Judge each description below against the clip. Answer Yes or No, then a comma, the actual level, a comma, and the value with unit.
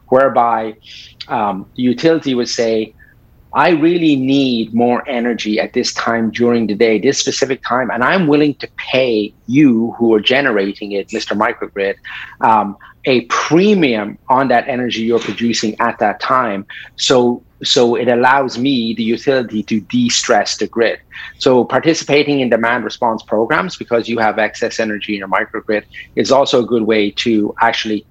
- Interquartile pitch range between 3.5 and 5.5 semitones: No, average, 3.1 semitones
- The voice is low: Yes, low, 115 Hz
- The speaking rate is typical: Yes, average, 160 wpm